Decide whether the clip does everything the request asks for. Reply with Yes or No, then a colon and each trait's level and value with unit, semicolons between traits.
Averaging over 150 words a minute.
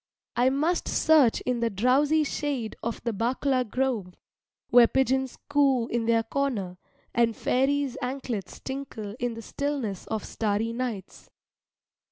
No: slow, 135 wpm